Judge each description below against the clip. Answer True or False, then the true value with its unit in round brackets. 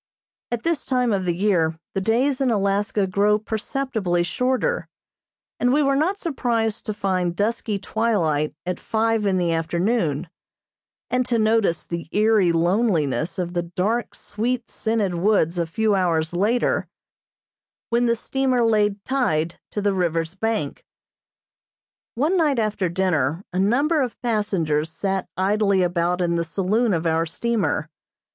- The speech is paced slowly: False (145 wpm)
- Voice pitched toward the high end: True (205 Hz)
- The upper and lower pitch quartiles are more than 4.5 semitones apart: True (5.1 semitones)